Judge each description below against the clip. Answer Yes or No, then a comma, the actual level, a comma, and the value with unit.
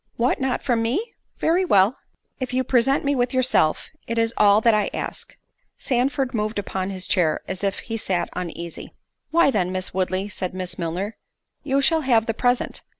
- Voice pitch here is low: No, high, 225 Hz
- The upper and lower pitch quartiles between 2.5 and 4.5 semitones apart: No, wide, 5.6 semitones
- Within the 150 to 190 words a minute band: Yes, average, 185 wpm